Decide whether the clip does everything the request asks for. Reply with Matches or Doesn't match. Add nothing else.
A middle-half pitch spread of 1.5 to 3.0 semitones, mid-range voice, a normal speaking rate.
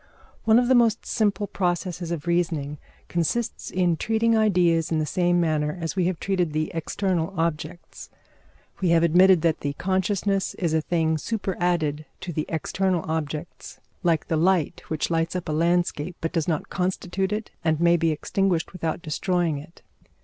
Matches